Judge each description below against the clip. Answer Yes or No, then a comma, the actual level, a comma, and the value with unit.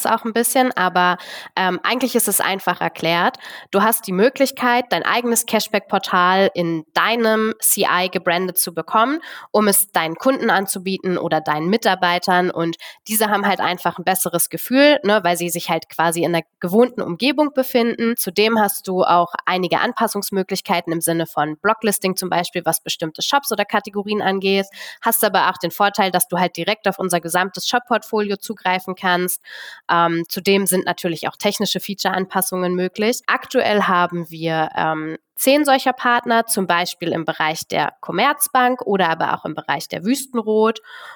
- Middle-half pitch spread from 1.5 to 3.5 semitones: No, average, 4.3 semitones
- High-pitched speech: Yes, high, 195 Hz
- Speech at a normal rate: Yes, average, 160 wpm